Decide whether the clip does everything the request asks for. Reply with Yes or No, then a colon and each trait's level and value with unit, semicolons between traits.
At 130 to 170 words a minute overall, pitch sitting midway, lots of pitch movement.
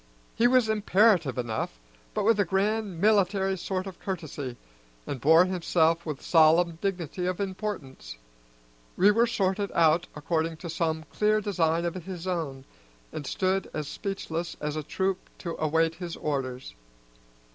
No: average, 145 wpm; medium, 175 Hz; average, 3.5 semitones